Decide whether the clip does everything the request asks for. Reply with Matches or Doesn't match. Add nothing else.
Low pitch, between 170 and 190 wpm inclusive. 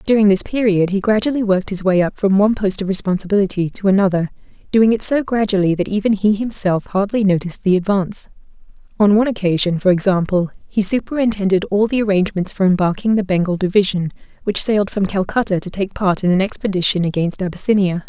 Doesn't match